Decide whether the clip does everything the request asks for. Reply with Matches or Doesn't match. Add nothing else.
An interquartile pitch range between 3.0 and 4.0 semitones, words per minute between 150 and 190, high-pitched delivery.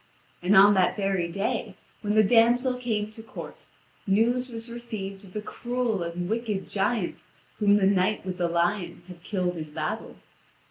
Matches